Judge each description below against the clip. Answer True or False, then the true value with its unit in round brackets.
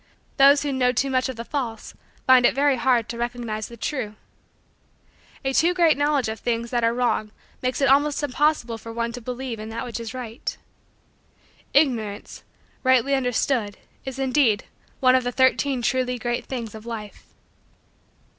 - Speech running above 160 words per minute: True (170 wpm)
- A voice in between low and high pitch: False (250 Hz)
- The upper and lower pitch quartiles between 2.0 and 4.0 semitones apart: True (2.6 semitones)